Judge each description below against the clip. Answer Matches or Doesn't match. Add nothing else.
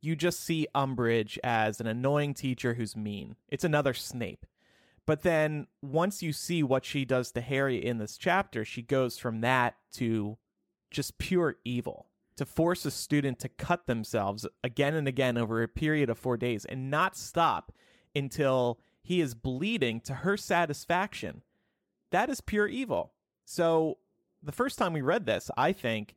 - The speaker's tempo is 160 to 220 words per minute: Matches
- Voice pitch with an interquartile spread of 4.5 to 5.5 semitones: Matches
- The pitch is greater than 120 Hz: Matches